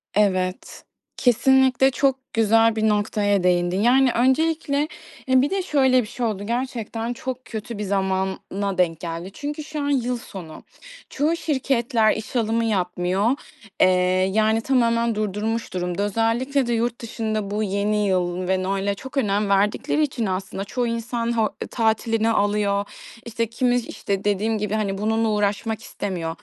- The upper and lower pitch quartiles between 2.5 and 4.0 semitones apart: Yes, average, 3.6 semitones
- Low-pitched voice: No, high, 220 Hz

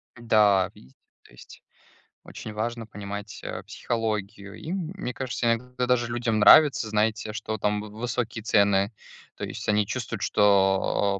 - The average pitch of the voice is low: Yes, low, 110 Hz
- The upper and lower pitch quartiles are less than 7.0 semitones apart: Yes, average, 2.7 semitones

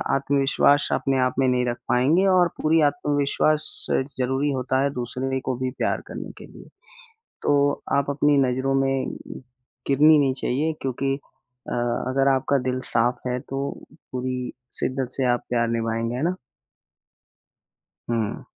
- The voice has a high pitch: No, low, 135 Hz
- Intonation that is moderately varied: No, narrow, 2.1 semitones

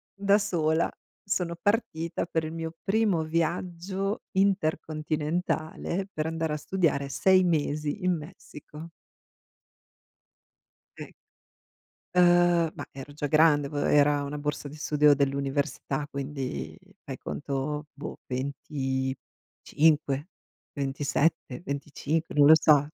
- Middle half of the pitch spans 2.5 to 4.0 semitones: Yes, average, 2.9 semitones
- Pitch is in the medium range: Yes, medium, 155 Hz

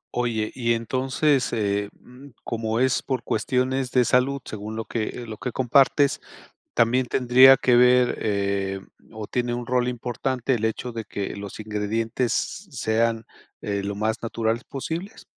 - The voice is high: No, low, 120 Hz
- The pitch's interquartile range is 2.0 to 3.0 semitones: Yes, average, 2.7 semitones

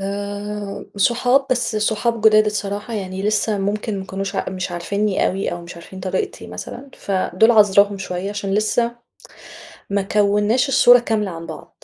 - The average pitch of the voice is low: No, high, 205 Hz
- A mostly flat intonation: Yes, narrow, 2.1 semitones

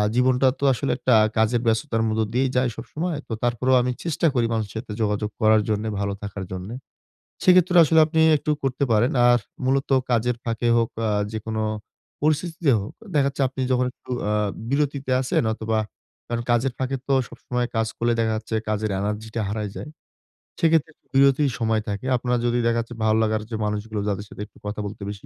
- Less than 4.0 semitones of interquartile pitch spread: Yes, average, 3.6 semitones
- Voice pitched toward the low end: Yes, low, 120 Hz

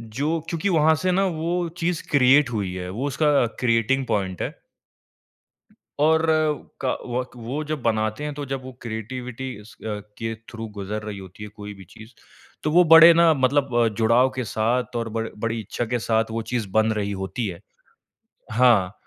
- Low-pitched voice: Yes, low, 120 Hz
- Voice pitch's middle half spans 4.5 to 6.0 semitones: Yes, average, 4.9 semitones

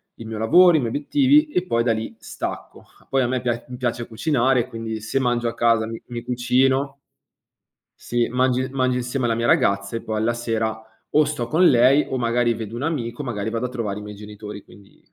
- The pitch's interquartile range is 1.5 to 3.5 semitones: Yes, narrow, 2.5 semitones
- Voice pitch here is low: Yes, low, 120 Hz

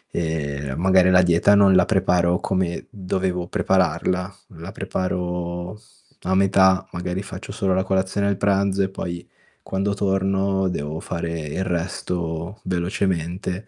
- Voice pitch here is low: Yes, very low, 90 Hz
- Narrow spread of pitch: Yes, narrow, 1.8 semitones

